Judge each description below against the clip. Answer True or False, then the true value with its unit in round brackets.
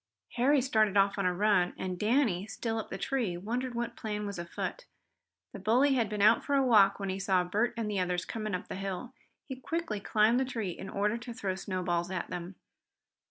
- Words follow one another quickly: True (215 wpm)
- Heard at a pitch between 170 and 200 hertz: False (210 Hz)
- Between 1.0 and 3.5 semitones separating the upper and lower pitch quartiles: False (4.1 semitones)